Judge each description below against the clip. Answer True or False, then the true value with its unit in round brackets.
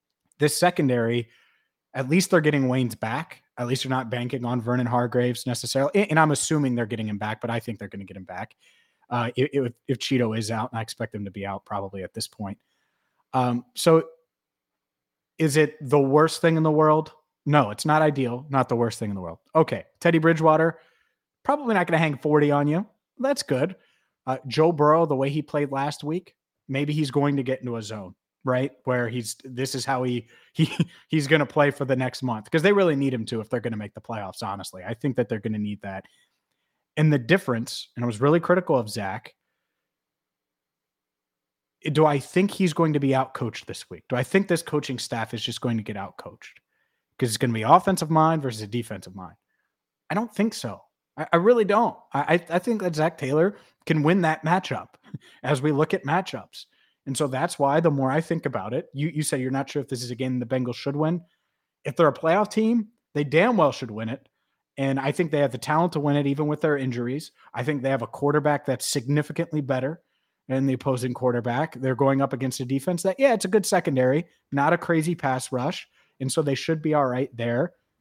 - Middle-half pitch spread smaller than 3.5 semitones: False (4.5 semitones)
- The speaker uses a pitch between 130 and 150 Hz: True (140 Hz)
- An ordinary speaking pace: False (225 wpm)